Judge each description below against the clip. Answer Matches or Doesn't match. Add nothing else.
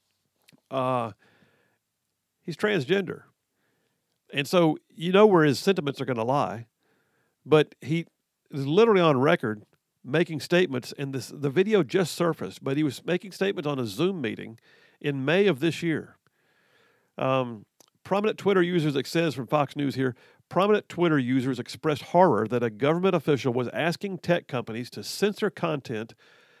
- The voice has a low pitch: Doesn't match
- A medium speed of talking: Matches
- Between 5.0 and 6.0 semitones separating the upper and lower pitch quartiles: Matches